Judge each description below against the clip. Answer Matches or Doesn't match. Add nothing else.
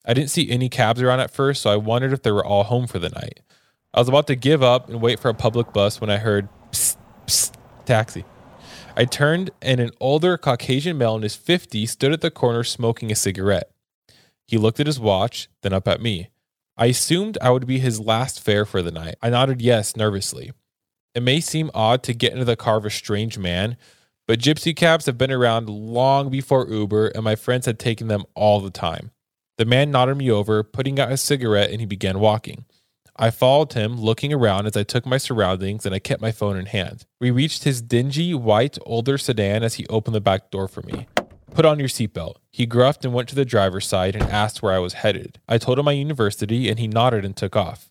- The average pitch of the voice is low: Matches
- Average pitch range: Matches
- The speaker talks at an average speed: Doesn't match